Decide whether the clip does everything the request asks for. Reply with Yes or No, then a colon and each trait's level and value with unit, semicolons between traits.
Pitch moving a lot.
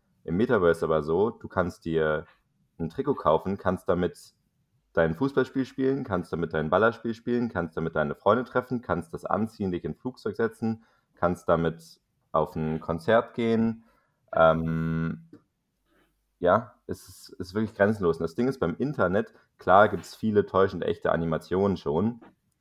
Yes: wide, 5.7 semitones